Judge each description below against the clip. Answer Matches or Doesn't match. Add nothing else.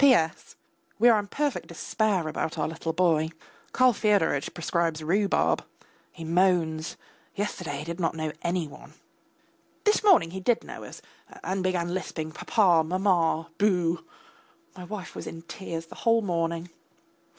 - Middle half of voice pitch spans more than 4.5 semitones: Doesn't match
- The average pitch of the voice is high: Doesn't match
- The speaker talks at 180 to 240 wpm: Doesn't match